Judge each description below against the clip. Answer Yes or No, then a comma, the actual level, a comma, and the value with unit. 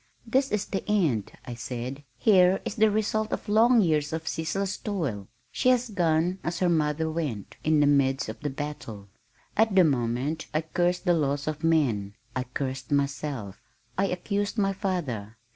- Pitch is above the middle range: No, medium, 160 Hz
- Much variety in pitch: Yes, wide, 6.5 semitones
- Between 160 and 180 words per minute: Yes, average, 175 wpm